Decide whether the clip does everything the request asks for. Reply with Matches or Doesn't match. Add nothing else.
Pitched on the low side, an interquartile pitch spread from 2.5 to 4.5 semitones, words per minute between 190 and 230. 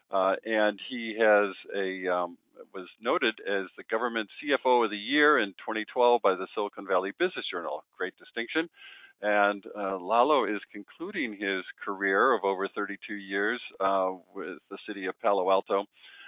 Doesn't match